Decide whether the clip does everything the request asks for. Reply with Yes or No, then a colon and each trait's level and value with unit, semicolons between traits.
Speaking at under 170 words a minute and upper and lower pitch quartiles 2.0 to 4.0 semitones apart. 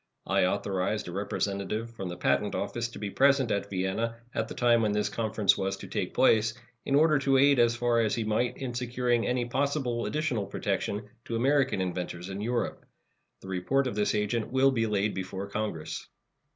No: average, 190 wpm; average, 3.6 semitones